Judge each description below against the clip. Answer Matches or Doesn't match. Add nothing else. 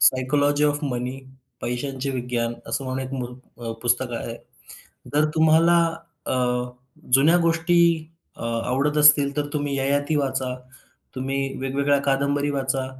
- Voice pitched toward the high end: Doesn't match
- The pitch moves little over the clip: Matches